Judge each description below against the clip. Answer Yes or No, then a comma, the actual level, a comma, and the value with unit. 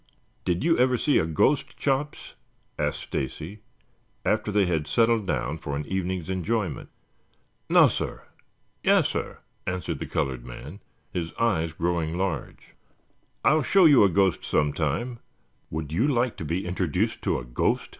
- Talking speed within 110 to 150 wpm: Yes, average, 145 wpm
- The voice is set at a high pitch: No, very low, 90 Hz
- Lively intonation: Yes, wide, 6.7 semitones